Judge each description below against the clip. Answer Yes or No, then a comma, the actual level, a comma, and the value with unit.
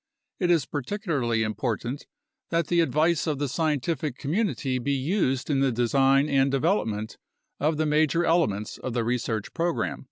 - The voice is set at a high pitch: No, medium, 140 Hz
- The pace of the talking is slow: No, average, 155 wpm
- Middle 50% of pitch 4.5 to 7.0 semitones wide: Yes, average, 4.8 semitones